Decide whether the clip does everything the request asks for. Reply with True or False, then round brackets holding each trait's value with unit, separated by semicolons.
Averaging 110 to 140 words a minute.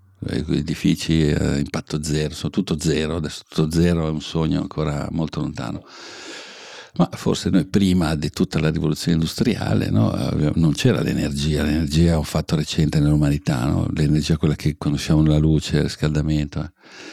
False (160 wpm)